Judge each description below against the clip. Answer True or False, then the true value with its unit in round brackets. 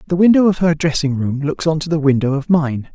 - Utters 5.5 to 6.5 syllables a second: True (5.8 syllables/s)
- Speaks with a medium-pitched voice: True (155 Hz)